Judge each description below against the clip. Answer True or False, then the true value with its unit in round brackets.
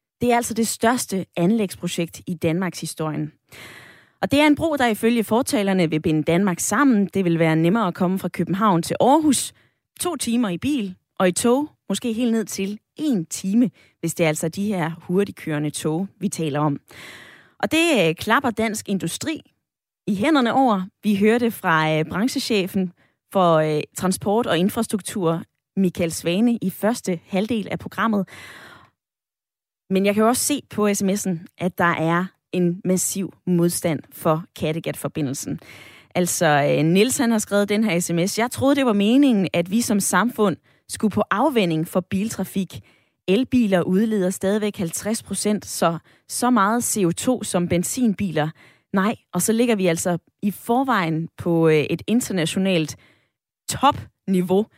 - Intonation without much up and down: False (4.9 semitones)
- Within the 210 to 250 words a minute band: False (150 wpm)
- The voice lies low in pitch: False (190 Hz)